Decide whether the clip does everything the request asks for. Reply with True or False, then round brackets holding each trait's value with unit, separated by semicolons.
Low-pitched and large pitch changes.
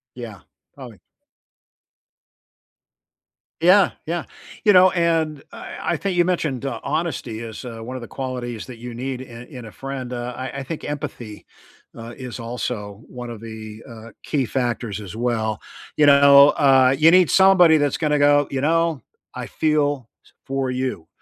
False (130 Hz; 4.3 semitones)